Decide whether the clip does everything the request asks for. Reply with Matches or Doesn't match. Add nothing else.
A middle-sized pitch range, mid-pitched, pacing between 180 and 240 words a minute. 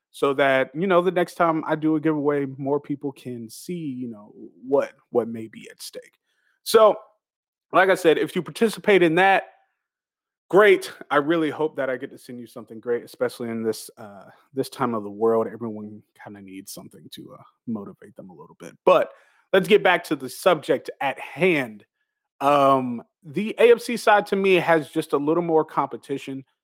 Doesn't match